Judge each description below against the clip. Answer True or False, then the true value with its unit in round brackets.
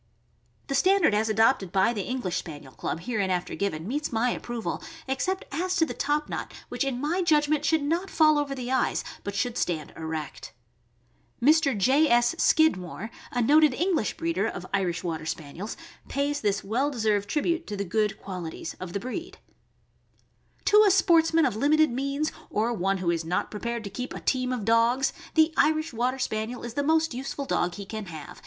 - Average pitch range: False (7.0 semitones)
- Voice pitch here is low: False (240 Hz)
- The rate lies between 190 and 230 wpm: True (195 wpm)